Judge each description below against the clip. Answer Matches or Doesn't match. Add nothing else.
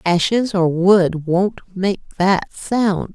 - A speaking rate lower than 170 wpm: Matches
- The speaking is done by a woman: Matches